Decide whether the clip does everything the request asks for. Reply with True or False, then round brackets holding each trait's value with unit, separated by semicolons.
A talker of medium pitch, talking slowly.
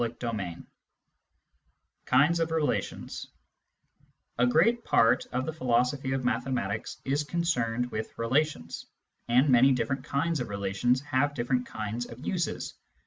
False (125 Hz; 130 wpm)